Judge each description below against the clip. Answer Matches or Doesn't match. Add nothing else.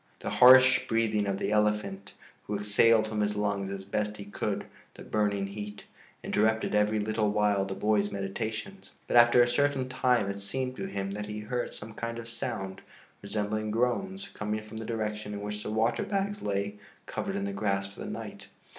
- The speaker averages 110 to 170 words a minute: Doesn't match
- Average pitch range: Doesn't match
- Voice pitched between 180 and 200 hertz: Doesn't match